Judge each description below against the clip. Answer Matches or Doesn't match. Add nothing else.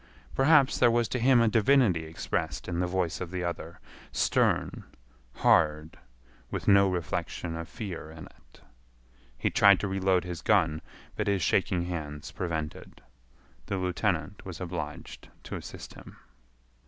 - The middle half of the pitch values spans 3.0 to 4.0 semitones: Matches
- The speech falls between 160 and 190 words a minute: Doesn't match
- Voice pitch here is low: Matches